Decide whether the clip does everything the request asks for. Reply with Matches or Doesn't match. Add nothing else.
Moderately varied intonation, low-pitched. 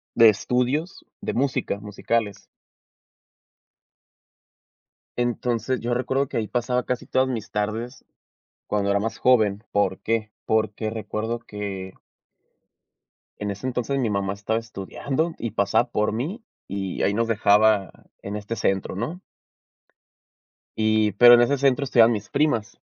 Matches